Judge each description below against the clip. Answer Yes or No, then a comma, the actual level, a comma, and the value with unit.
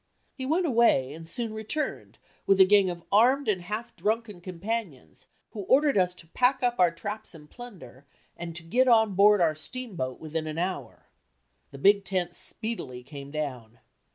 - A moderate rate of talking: Yes, average, 175 wpm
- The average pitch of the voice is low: No, high, 190 Hz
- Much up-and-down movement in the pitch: Yes, wide, 6.1 semitones